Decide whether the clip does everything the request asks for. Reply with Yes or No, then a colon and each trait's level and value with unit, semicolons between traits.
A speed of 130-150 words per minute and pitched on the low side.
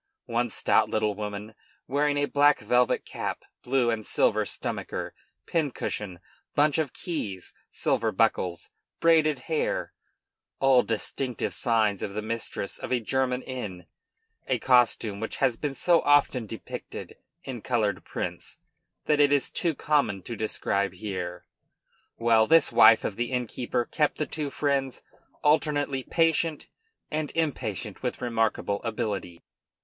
Yes: slow, 135 wpm; low, 125 Hz